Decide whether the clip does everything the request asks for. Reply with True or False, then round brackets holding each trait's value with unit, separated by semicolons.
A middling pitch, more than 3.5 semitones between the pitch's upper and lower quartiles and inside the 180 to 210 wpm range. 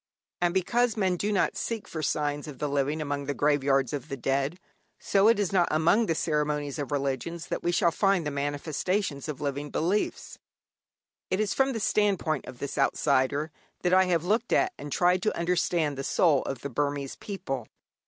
True (155 Hz; 4.8 semitones; 195 wpm)